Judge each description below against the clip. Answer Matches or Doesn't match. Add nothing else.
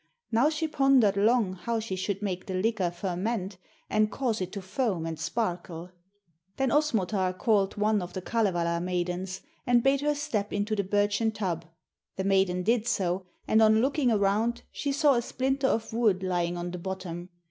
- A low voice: Doesn't match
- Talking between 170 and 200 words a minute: Matches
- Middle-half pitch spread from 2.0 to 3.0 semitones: Doesn't match